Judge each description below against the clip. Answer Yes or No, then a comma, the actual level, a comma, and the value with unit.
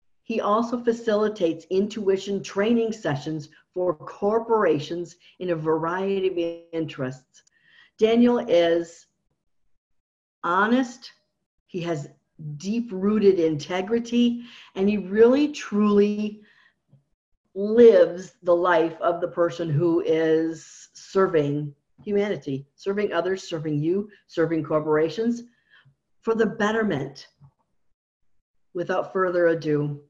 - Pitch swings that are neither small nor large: Yes, average, 4.6 semitones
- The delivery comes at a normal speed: No, slow, 95 wpm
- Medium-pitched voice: Yes, medium, 180 Hz